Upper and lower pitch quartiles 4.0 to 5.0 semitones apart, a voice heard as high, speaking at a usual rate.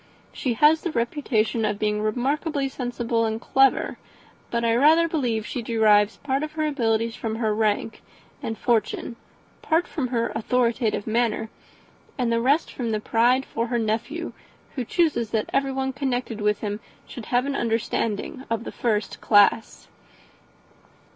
No: average, 3.3 semitones; high, 235 Hz; average, 155 wpm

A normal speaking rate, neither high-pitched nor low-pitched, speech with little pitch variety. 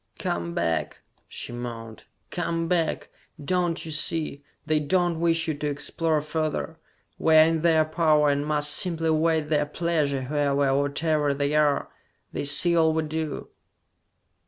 Yes: average, 155 wpm; medium, 155 Hz; narrow, 2.3 semitones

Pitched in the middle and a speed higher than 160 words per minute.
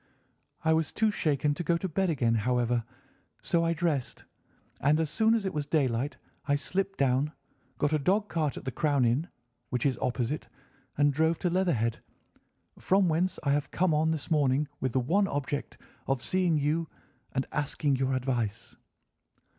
Yes: medium, 150 Hz; average, 175 wpm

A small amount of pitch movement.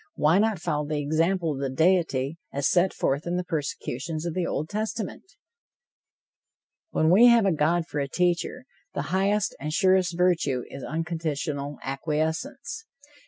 No: average, 4.1 semitones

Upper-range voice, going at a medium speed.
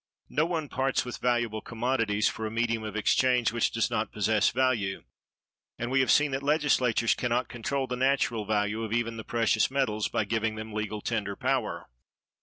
No: low, 115 Hz; average, 190 wpm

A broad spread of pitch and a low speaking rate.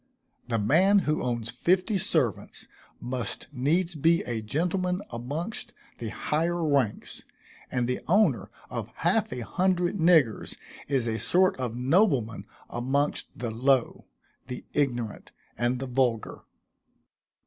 Yes: wide, 6.3 semitones; slow, 125 wpm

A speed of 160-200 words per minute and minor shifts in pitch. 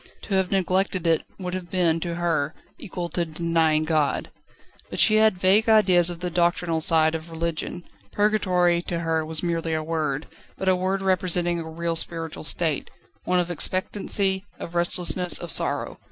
Yes: average, 170 wpm; narrow, 2.2 semitones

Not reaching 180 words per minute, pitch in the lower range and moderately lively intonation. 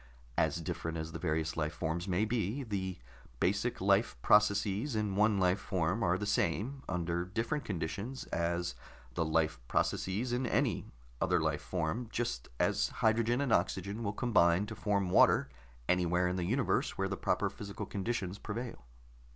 Yes: average, 160 wpm; very low, 95 Hz; average, 4.4 semitones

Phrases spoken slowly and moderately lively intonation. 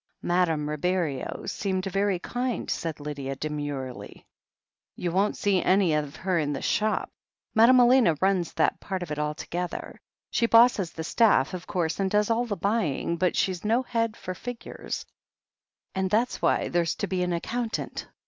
No: average, 165 wpm; average, 5.0 semitones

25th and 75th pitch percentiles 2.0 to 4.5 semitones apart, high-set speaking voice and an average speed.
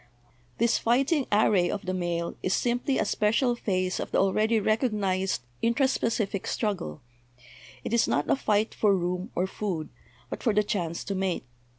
Yes: average, 3.7 semitones; high, 205 Hz; average, 170 wpm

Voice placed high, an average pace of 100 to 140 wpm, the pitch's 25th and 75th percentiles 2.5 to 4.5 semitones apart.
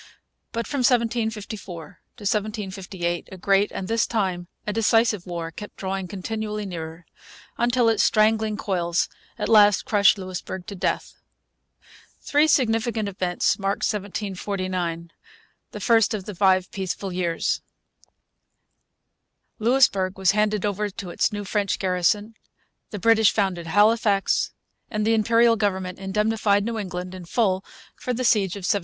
Yes: high, 205 Hz; slow, 135 wpm; average, 2.9 semitones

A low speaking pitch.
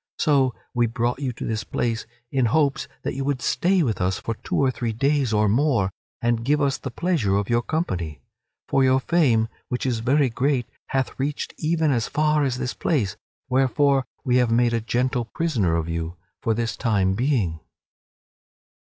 Yes: low, 125 Hz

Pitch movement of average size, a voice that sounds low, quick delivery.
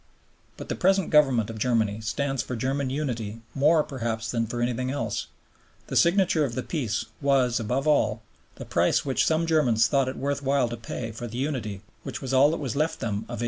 Yes: average, 3.8 semitones; low, 130 Hz; fast, 210 wpm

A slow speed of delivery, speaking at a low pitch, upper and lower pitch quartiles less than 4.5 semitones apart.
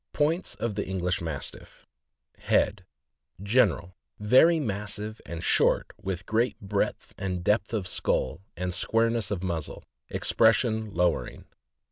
Yes: slow, 125 wpm; low, 100 Hz; average, 3.8 semitones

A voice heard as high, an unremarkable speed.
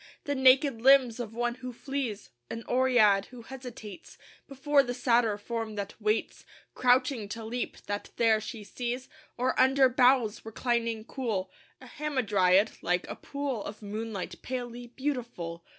Yes: high, 240 Hz; average, 145 wpm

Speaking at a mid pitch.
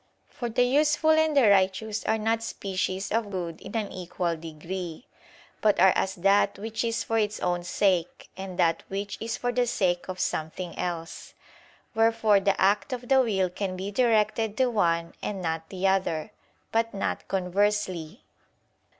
No: high, 200 Hz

